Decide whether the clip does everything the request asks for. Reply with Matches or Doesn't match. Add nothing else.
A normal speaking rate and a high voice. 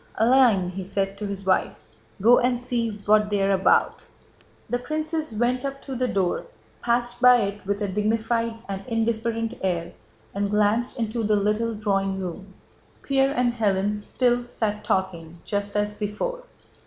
Matches